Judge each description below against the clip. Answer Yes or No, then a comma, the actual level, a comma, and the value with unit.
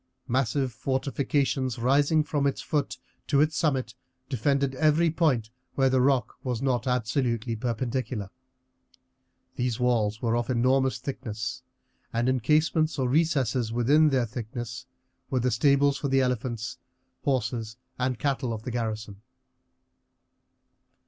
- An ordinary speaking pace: No, slow, 130 wpm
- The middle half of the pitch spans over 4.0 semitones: No, average, 3.0 semitones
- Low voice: Yes, low, 130 Hz